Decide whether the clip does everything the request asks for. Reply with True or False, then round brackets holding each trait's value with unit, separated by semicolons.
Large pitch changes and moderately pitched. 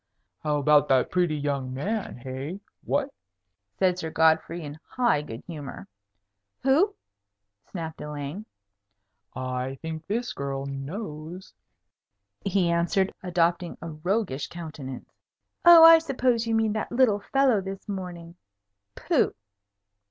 True (6.1 semitones; 170 Hz)